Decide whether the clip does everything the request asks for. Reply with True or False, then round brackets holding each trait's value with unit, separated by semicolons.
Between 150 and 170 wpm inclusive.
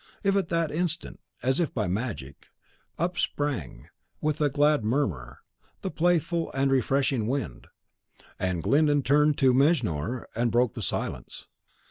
False (135 wpm)